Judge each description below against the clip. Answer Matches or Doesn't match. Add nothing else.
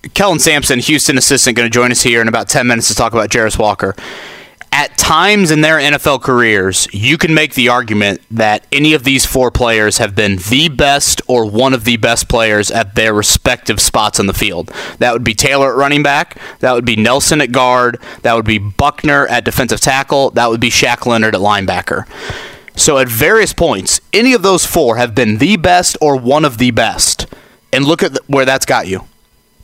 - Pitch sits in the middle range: Doesn't match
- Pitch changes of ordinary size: Matches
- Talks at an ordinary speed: Doesn't match